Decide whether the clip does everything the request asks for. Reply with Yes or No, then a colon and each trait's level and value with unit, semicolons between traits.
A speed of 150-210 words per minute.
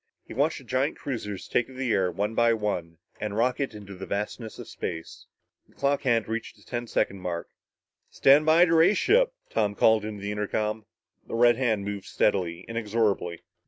Yes: average, 190 wpm